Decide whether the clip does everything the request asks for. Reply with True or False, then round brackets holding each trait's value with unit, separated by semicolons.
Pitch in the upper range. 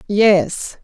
True (200 Hz)